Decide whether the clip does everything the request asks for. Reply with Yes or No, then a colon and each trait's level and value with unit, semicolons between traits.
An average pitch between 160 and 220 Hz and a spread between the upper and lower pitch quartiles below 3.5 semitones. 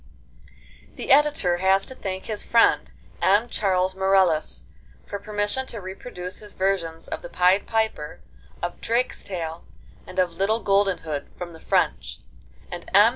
Yes: high, 190 Hz; average, 2.7 semitones